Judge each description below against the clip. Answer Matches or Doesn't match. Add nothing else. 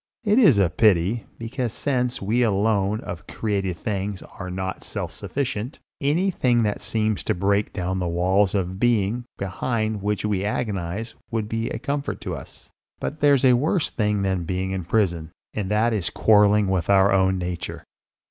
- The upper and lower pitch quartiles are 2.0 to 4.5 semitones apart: Matches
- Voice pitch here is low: Matches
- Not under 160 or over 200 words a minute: Matches